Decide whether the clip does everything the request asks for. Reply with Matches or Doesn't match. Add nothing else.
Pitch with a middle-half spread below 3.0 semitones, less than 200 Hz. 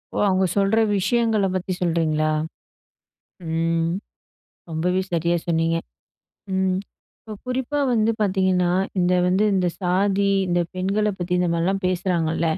Matches